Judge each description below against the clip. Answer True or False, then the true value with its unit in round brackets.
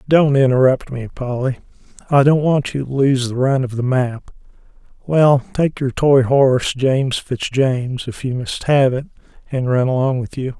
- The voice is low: True (130 Hz)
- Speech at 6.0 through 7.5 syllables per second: False (4.7 syllables/s)